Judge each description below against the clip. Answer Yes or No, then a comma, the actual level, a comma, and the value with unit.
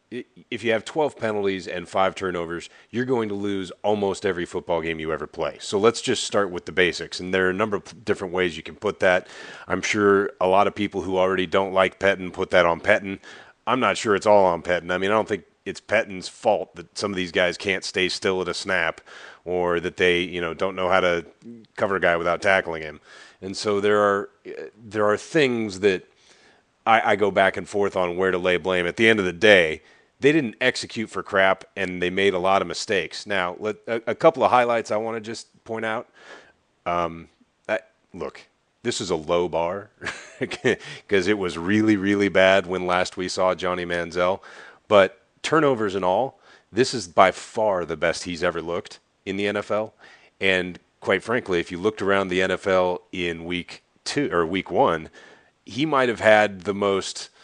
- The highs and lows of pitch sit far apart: No, narrow, 2.5 semitones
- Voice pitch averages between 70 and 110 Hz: Yes, very low, 95 Hz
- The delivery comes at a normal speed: No, fast, 210 wpm